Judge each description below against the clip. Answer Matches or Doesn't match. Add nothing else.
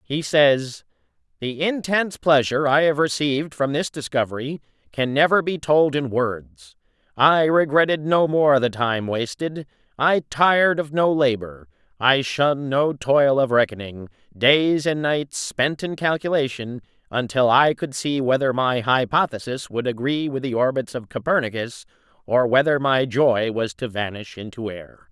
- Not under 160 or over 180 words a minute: Doesn't match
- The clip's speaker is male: Matches